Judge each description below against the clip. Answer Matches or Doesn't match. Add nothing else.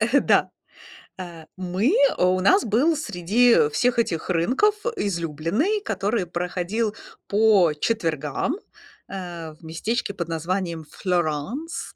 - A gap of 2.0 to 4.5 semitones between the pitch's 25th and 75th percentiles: Doesn't match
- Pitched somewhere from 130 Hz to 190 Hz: Matches